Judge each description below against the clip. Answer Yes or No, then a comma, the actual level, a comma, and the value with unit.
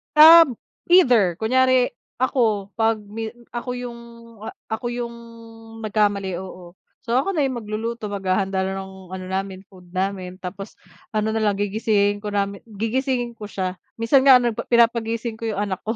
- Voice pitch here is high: Yes, high, 215 Hz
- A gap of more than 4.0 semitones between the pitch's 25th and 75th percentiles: No, average, 3.4 semitones